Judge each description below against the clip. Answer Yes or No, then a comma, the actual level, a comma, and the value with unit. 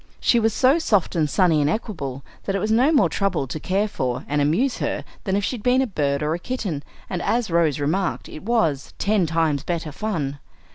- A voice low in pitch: No, medium, 180 Hz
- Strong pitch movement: Yes, wide, 6.5 semitones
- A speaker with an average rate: No, fast, 225 wpm